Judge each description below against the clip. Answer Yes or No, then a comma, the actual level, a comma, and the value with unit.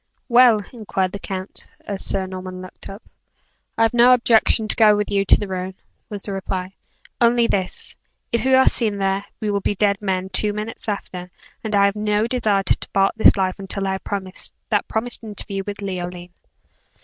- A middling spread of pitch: No, narrow, 2.3 semitones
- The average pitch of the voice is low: No, high, 200 Hz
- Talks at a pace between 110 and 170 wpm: No, average, 195 wpm